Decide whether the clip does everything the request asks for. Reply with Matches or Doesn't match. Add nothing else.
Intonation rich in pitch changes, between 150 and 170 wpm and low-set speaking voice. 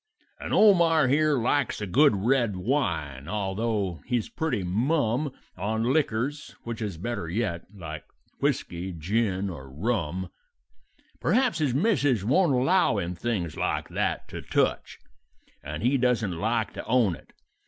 Doesn't match